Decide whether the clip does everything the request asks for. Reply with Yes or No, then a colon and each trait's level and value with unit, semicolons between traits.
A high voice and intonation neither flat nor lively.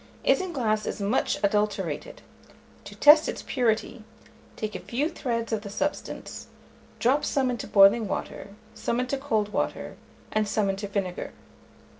Yes: high, 220 Hz; average, 3.6 semitones